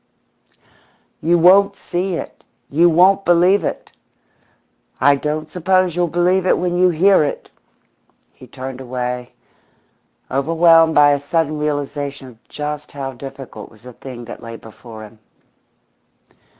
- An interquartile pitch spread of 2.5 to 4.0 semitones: No, average, 4.8 semitones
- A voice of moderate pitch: Yes, medium, 150 Hz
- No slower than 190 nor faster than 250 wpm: No, slow, 135 wpm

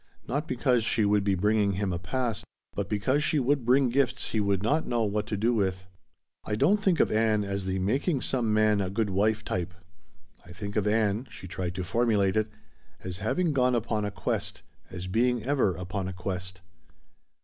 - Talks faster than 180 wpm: Yes, average, 200 wpm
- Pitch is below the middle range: Yes, low, 105 Hz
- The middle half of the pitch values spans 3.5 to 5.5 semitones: Yes, average, 4.2 semitones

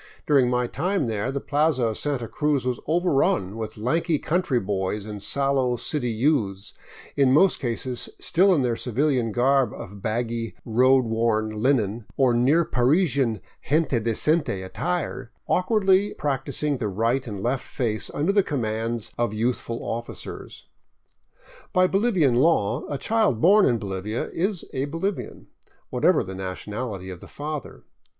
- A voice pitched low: Yes, low, 125 Hz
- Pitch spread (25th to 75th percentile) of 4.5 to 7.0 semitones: Yes, average, 5.1 semitones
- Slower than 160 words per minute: Yes, average, 145 wpm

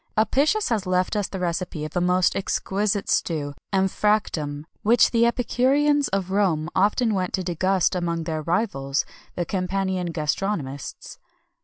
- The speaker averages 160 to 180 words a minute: No, average, 140 wpm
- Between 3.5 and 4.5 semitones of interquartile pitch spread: Yes, average, 3.9 semitones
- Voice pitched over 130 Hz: Yes, medium, 185 Hz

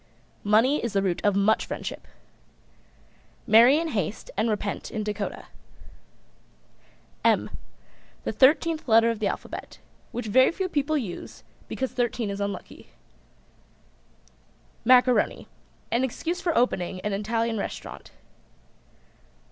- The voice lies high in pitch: Yes, high, 225 Hz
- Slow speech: Yes, slow, 125 wpm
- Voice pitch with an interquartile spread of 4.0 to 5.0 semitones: Yes, average, 4.3 semitones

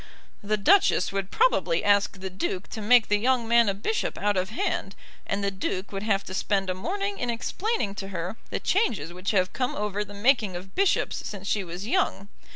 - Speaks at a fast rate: Yes, fast, 210 wpm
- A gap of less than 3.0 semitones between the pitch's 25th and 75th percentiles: No, average, 3.5 semitones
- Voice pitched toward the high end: Yes, high, 205 Hz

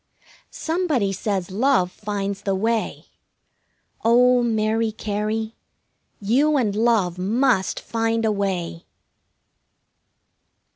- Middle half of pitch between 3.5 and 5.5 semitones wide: No, average, 3.0 semitones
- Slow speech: Yes, slow, 90 wpm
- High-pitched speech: Yes, high, 220 Hz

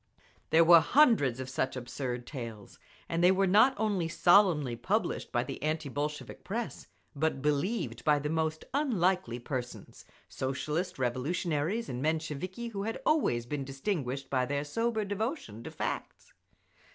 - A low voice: No, medium, 155 Hz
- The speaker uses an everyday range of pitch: No, wide, 6.5 semitones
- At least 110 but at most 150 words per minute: Yes, average, 140 wpm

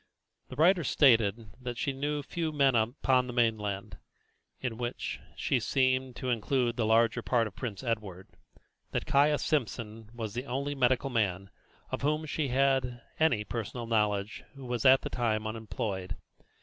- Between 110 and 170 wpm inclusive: Yes, average, 160 wpm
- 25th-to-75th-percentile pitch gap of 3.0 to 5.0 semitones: Yes, average, 3.5 semitones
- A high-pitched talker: No, low, 120 Hz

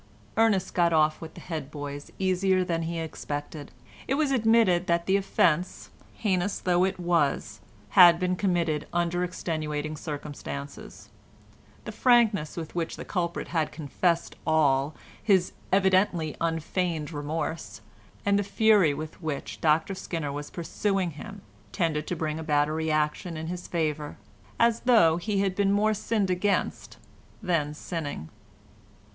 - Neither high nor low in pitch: Yes, medium, 170 Hz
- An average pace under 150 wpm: Yes, average, 140 wpm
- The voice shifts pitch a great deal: No, average, 3.7 semitones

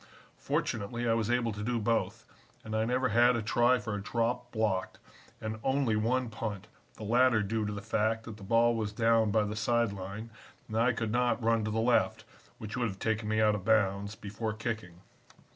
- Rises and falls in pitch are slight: Yes, narrow, 1.9 semitones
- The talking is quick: Yes, fast, 210 wpm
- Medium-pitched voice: No, low, 110 Hz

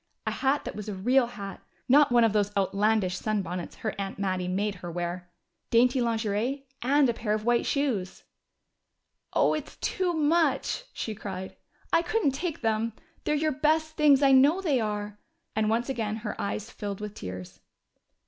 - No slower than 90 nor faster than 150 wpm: No, average, 175 wpm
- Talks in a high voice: Yes, high, 220 Hz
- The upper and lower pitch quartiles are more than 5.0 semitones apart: Yes, wide, 5.4 semitones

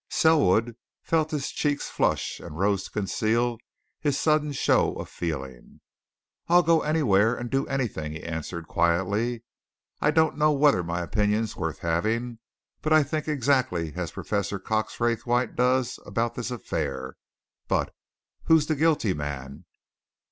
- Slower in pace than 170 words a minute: Yes, average, 140 wpm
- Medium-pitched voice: No, low, 115 Hz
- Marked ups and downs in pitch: Yes, wide, 8.2 semitones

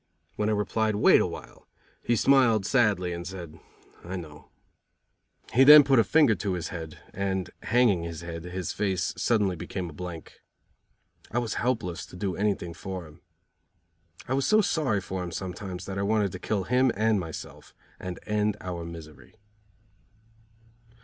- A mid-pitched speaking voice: No, very low, 95 Hz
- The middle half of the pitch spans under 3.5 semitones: No, average, 3.9 semitones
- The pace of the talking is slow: No, average, 165 wpm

